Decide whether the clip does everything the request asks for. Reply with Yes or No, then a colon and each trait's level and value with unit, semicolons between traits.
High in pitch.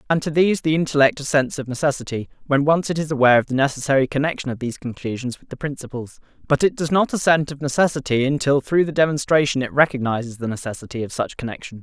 No: medium, 140 Hz